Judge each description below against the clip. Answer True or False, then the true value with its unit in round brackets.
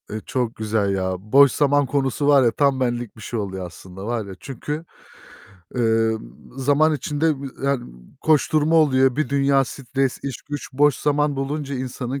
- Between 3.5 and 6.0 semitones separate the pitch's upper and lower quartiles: True (3.8 semitones)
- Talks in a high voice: False (135 Hz)